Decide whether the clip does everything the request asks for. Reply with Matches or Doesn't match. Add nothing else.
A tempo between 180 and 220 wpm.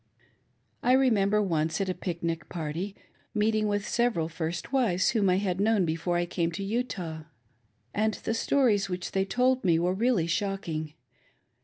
Doesn't match